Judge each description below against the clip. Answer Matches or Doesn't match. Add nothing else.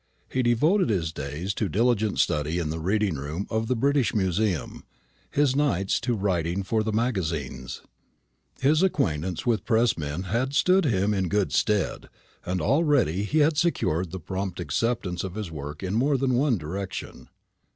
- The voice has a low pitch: Matches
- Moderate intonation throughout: Doesn't match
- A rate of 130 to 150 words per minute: Doesn't match